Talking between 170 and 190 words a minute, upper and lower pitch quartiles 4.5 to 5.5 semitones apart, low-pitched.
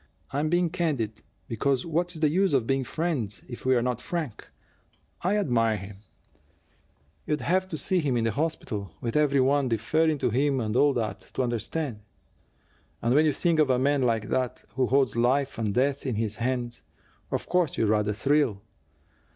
Yes: average, 180 wpm; average, 4.9 semitones; low, 130 Hz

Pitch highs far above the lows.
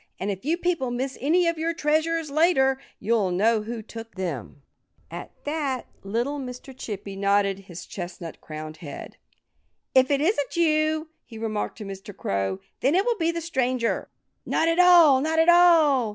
Yes: wide, 8.0 semitones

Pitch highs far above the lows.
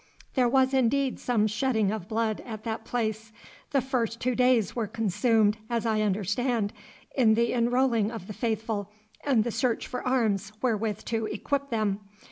No: narrow, 2.5 semitones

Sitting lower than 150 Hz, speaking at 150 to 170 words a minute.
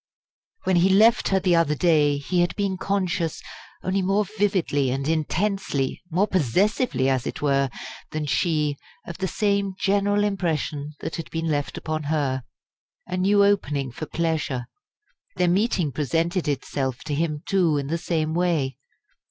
No: medium, 165 Hz; average, 155 wpm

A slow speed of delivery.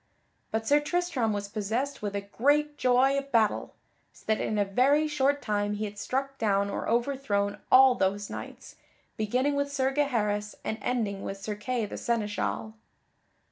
No: average, 170 wpm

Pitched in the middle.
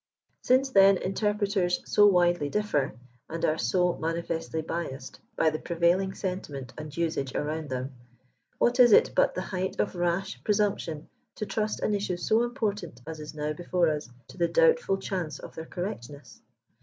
Yes: medium, 175 Hz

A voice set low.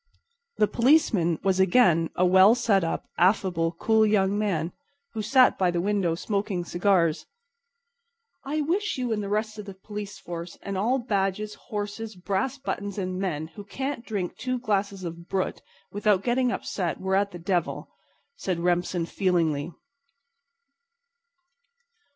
No: high, 195 Hz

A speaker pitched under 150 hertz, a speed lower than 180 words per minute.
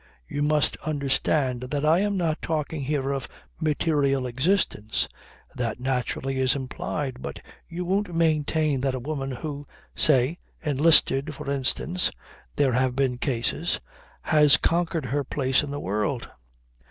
Yes: medium, 140 Hz; average, 140 wpm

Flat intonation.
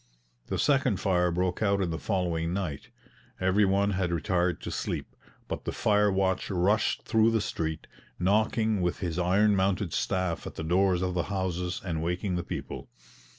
Yes: narrow, 2.3 semitones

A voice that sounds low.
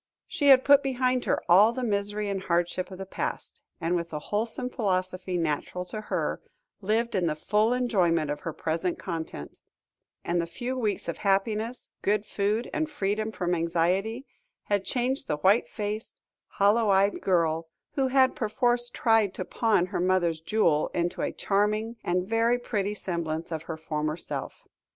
No: high, 200 Hz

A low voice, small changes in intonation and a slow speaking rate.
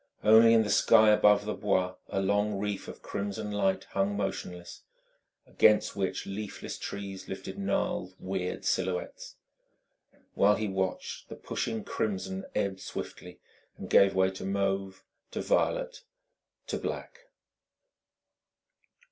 Yes: low, 100 Hz; narrow, 1.6 semitones; slow, 125 wpm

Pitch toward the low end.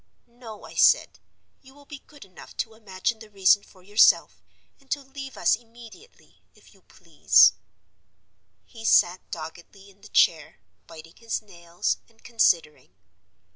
No: high, 220 Hz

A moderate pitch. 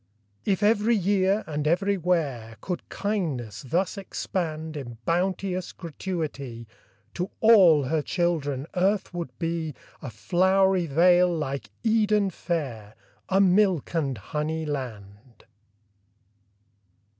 Yes: medium, 170 Hz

